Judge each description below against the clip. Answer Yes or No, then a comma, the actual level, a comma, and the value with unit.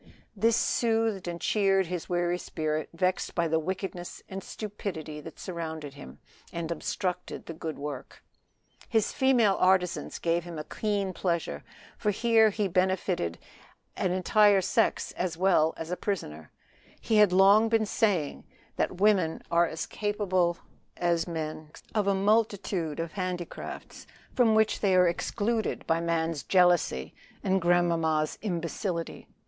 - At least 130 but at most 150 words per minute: Yes, average, 140 wpm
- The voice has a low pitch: No, medium, 180 Hz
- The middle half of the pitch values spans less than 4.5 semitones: Yes, average, 3.6 semitones